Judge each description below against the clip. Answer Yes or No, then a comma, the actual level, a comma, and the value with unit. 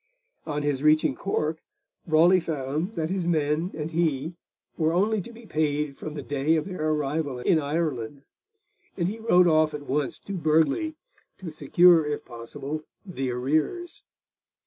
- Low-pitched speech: No, medium, 155 Hz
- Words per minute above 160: No, average, 155 wpm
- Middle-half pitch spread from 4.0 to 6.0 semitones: No, average, 3.0 semitones